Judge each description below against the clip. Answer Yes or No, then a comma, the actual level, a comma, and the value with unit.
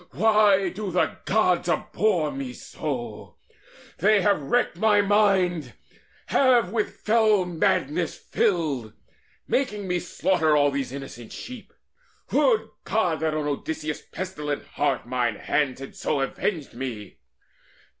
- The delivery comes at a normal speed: No, slow, 125 wpm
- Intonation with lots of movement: Yes, wide, 6.7 semitones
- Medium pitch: Yes, medium, 170 Hz